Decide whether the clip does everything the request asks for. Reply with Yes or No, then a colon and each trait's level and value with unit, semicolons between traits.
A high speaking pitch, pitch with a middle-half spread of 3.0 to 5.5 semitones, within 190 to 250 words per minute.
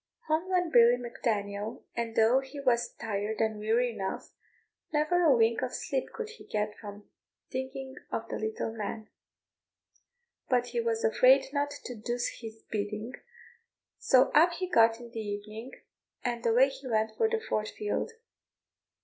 No: high, 235 Hz; average, 3.4 semitones; average, 160 wpm